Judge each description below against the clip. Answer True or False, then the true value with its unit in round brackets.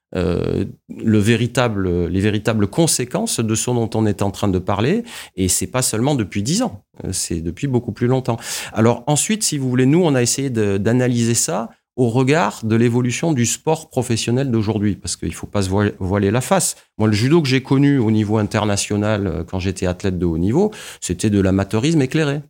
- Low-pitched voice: True (115 Hz)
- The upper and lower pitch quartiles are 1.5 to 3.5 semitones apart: False (4.3 semitones)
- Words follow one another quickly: False (200 wpm)